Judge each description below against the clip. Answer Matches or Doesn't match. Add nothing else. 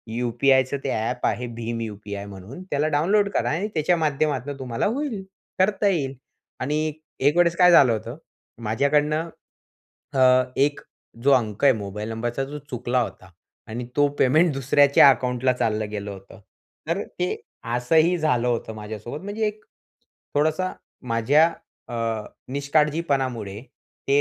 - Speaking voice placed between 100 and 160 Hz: Matches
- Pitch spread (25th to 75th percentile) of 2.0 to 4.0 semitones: Doesn't match